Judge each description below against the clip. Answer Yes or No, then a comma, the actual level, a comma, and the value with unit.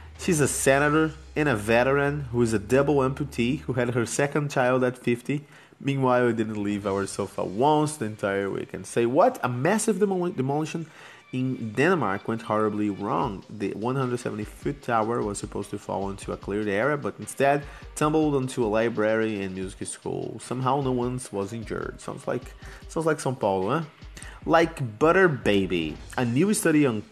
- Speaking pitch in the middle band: No, low, 125 Hz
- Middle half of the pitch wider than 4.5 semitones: Yes, average, 5.2 semitones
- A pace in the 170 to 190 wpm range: Yes, average, 175 wpm